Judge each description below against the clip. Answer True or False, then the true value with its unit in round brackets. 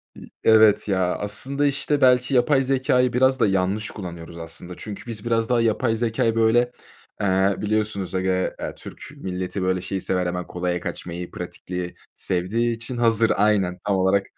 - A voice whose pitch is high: False (105 Hz)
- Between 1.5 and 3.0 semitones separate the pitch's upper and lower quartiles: False (4.4 semitones)